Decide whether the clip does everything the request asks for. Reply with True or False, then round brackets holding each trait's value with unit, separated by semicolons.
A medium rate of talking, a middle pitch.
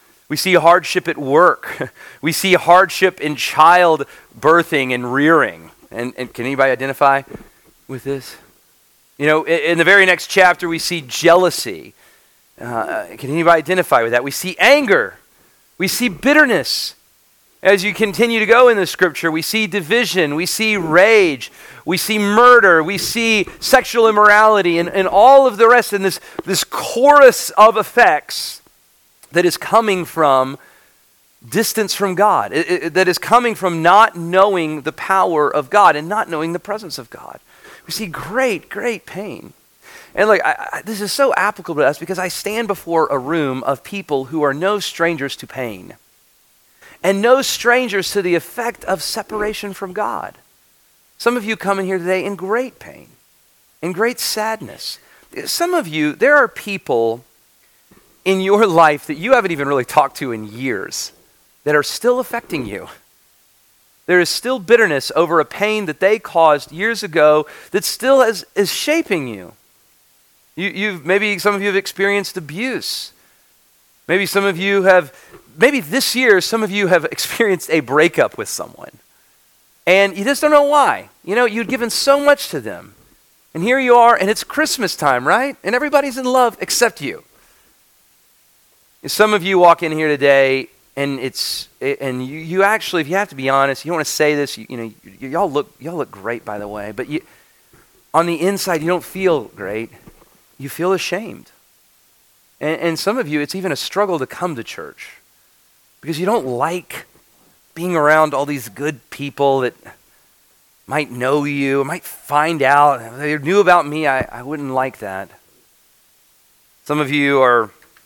True (175 wpm; 180 Hz)